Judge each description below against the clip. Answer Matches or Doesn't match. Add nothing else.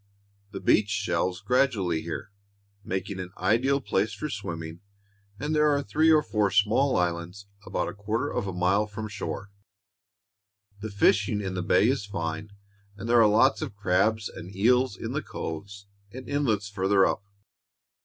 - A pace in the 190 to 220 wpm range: Doesn't match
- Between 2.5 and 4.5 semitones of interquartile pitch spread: Matches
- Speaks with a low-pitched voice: Matches